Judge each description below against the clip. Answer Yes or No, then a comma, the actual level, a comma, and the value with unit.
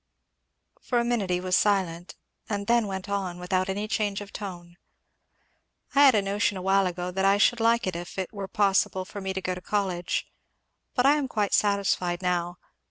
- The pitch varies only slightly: Yes, narrow, 2.3 semitones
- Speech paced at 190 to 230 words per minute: Yes, average, 195 wpm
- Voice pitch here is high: Yes, high, 195 Hz